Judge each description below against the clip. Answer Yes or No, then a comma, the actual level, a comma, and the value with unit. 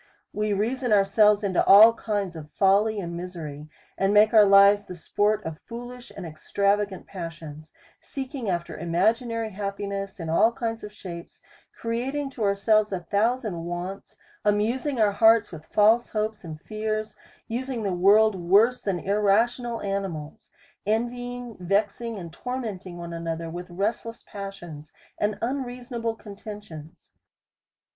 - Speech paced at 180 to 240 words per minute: No, average, 140 wpm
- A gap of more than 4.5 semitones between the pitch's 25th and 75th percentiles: No, average, 4.1 semitones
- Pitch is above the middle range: Yes, high, 205 Hz